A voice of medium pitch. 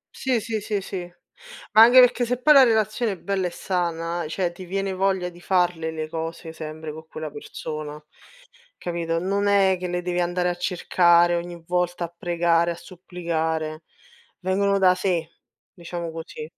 Yes: medium, 175 Hz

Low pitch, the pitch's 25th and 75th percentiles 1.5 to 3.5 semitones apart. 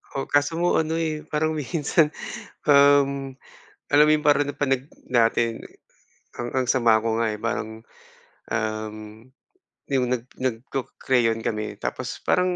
No: low, 130 Hz; average, 4.2 semitones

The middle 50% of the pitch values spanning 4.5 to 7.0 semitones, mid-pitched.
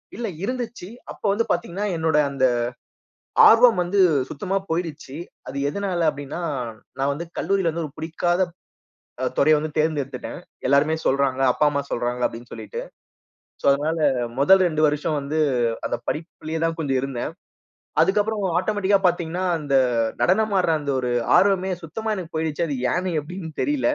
Yes: average, 4.8 semitones; medium, 165 Hz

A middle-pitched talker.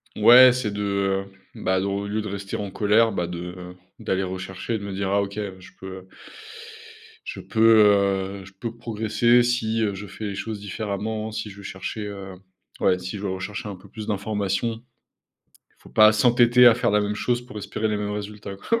No: low, 105 Hz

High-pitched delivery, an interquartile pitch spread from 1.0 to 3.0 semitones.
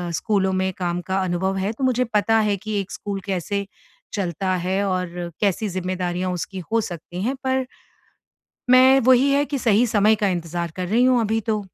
No: high, 200 Hz; average, 3.5 semitones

